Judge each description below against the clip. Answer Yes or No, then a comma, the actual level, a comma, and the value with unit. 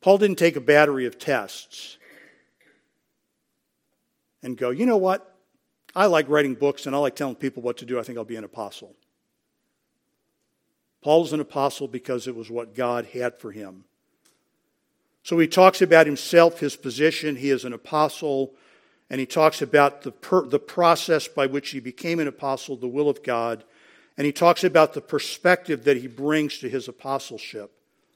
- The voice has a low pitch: No, medium, 145 Hz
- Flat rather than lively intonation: No, average, 3.6 semitones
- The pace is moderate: Yes, average, 175 wpm